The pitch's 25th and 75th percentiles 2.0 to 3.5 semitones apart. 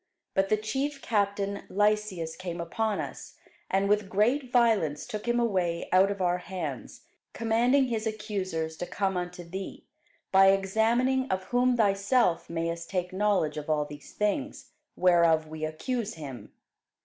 No: average, 4.5 semitones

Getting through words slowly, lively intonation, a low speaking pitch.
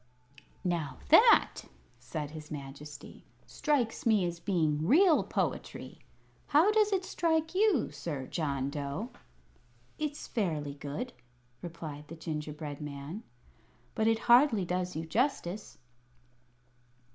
No: slow, 115 wpm; wide, 8.8 semitones; medium, 170 Hz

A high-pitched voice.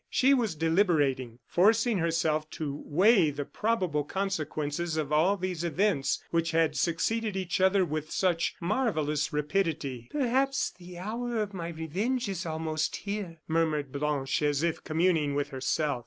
No: medium, 165 Hz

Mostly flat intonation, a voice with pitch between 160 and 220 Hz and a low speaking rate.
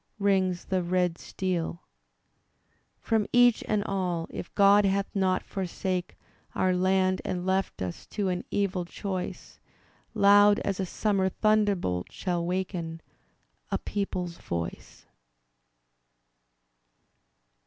Yes: narrow, 2.0 semitones; medium, 185 Hz; slow, 110 wpm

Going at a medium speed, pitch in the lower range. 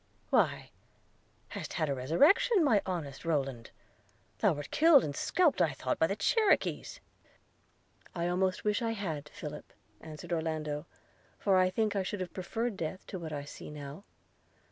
No: average, 165 wpm; medium, 175 Hz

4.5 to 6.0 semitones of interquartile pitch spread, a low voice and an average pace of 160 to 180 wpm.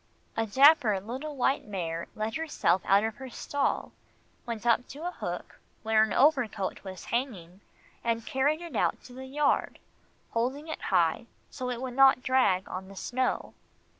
No: average, 5.0 semitones; high, 240 Hz; average, 165 wpm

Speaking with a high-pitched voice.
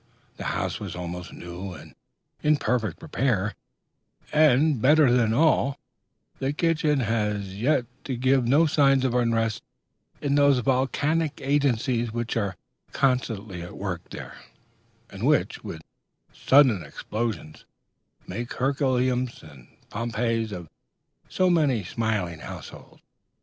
No: low, 120 Hz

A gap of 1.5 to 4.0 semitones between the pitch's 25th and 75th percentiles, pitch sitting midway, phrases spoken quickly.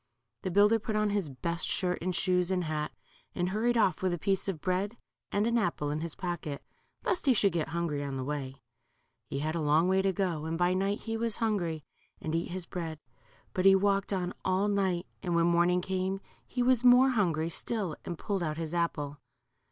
Yes: average, 3.5 semitones; medium, 180 Hz; fast, 215 wpm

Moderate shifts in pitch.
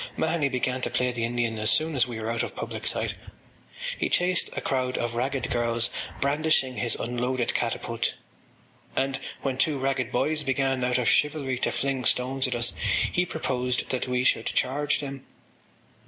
No: narrow, 2.0 semitones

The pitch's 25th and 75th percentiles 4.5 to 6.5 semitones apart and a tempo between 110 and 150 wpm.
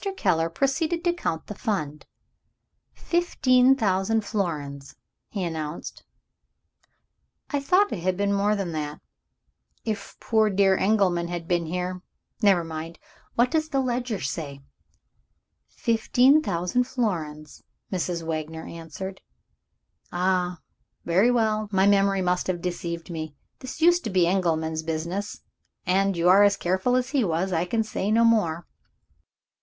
Yes: average, 4.9 semitones; average, 140 wpm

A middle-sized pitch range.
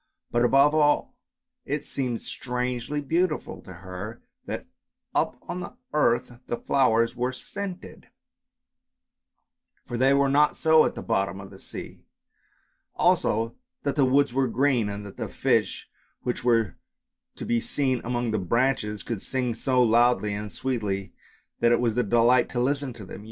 Yes: average, 3.3 semitones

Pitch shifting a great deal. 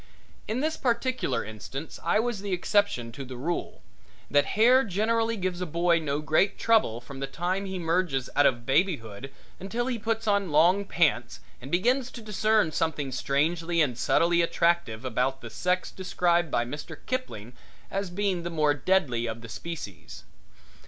Yes: wide, 6.8 semitones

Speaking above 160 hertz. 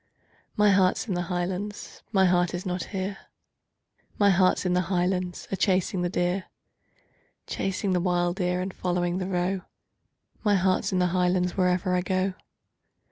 Yes: medium, 185 Hz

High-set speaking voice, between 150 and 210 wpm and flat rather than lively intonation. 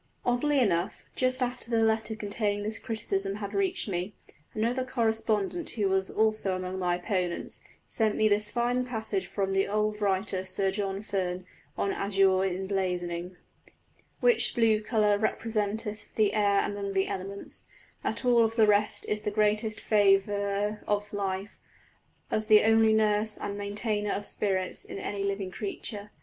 Yes: high, 205 Hz; average, 155 wpm; narrow, 2.1 semitones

